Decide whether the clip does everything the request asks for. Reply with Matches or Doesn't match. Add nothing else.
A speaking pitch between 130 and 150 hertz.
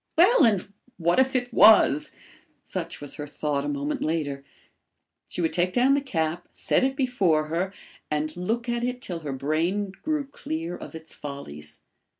Doesn't match